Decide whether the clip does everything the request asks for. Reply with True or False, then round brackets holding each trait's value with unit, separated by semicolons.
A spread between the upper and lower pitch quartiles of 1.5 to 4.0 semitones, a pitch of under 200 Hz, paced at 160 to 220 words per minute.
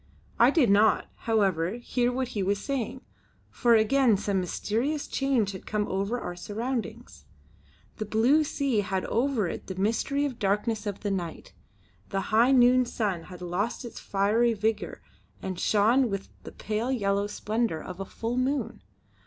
False (3.7 semitones; 220 Hz; 165 wpm)